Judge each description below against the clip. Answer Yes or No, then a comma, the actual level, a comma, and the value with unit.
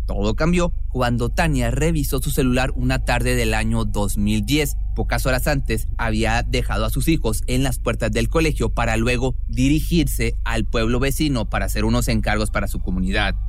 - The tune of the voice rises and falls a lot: No, average, 3.4 semitones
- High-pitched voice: No, low, 120 Hz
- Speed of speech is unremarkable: Yes, average, 170 wpm